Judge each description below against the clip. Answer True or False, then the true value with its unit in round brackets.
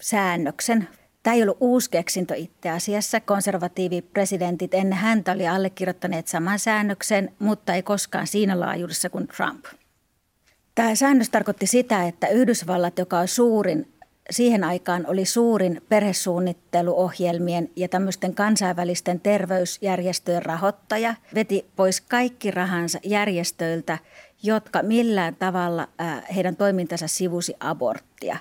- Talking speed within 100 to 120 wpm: True (110 wpm)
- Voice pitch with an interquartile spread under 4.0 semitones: True (2.9 semitones)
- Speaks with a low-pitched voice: False (185 Hz)